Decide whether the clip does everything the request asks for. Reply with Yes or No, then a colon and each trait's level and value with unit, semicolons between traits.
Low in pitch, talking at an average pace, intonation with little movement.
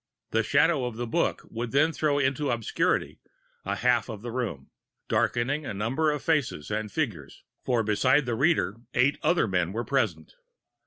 No: low, 120 Hz; average, 170 wpm; average, 5.0 semitones